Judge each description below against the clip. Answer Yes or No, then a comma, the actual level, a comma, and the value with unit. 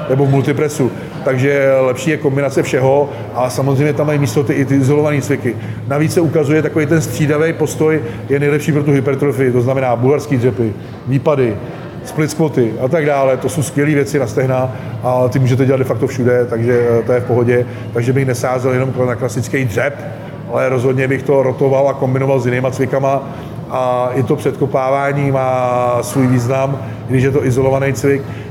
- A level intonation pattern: Yes, narrow, 2.1 semitones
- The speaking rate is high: Yes, fast, 180 wpm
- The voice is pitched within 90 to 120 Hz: No, low, 135 Hz